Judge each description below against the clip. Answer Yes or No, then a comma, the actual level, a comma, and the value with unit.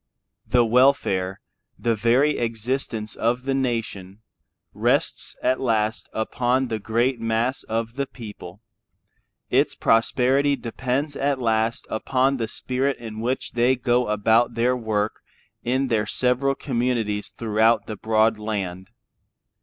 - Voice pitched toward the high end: No, low, 115 Hz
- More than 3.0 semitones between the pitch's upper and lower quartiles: No, narrow, 2.6 semitones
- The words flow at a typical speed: No, slow, 125 wpm